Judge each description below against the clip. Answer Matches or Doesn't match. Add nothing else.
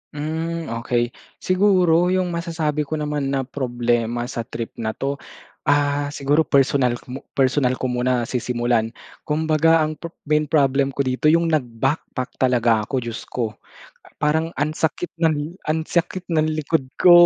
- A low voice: Doesn't match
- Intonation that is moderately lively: Matches